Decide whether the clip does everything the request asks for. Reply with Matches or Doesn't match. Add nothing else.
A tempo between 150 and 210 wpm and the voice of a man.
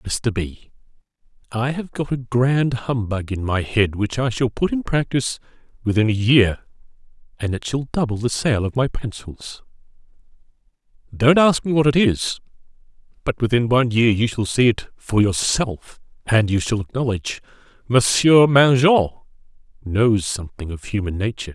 Matches